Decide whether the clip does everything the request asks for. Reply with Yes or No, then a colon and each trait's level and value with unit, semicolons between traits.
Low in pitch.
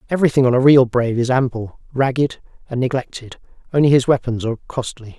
Yes: low, 125 Hz